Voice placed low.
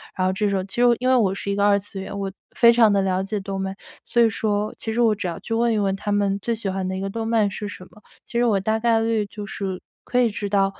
No: high, 205 Hz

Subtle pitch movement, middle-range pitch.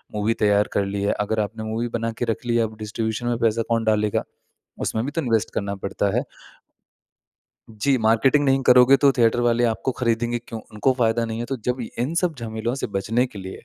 No: narrow, 2.1 semitones; low, 115 Hz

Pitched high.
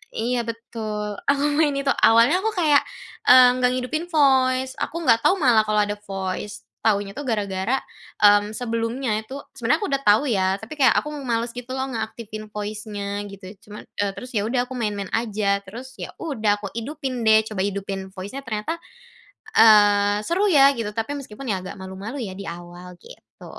Yes: high, 225 Hz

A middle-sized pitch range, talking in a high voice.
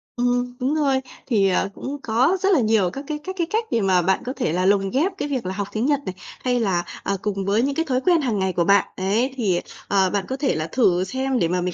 No: wide, 6.0 semitones; high, 230 Hz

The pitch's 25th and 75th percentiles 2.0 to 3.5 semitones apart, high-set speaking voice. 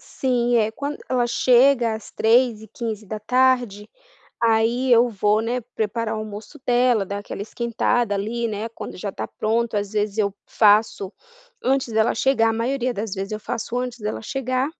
Yes: narrow, 2.5 semitones; high, 230 Hz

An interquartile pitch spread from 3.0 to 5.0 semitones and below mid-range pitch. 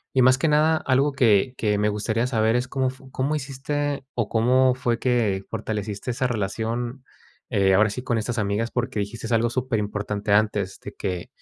Yes: average, 3.6 semitones; low, 120 Hz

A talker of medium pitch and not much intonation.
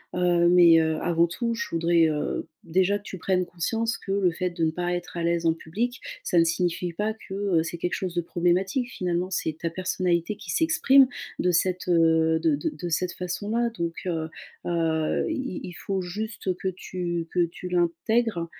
Yes: medium, 175 Hz; narrow, 2.2 semitones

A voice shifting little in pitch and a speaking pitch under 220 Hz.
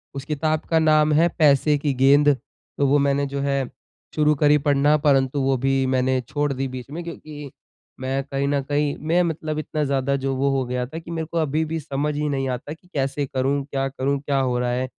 Yes: narrow, 1.9 semitones; medium, 140 Hz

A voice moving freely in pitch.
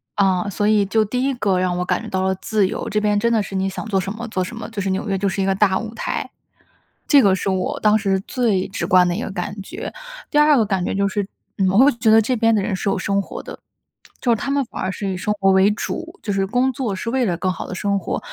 No: average, 3.0 semitones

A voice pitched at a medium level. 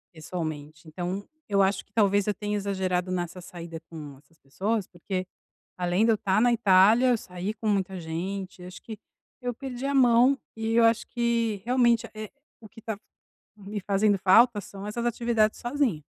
No: high, 205 Hz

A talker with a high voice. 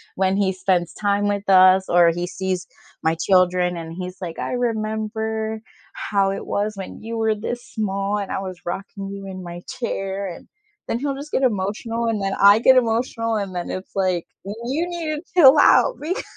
Yes: high, 200 Hz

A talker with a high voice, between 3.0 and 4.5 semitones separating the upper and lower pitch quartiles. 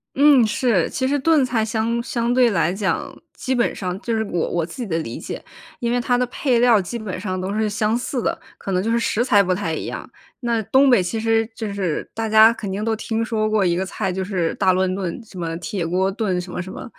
Yes: high, 215 Hz; average, 4.1 semitones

